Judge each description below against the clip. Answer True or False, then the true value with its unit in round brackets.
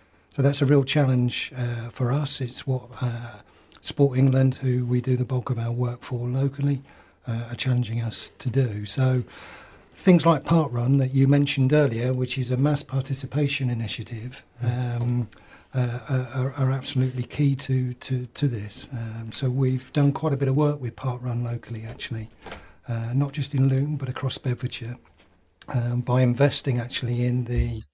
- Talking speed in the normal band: True (175 wpm)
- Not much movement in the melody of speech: True (2.1 semitones)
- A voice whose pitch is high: False (125 Hz)